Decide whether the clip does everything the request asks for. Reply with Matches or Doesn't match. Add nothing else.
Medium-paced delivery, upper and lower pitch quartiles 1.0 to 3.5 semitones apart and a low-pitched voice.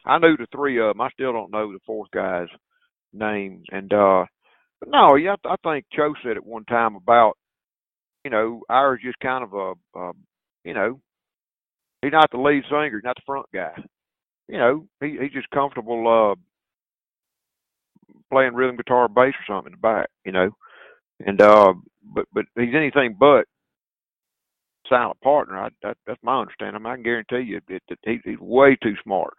Doesn't match